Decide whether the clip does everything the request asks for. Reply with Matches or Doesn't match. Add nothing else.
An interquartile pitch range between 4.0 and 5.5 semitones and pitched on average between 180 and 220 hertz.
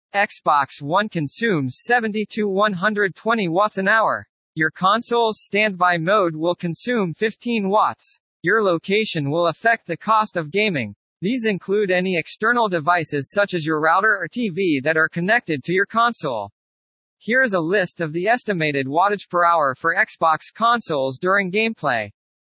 Matches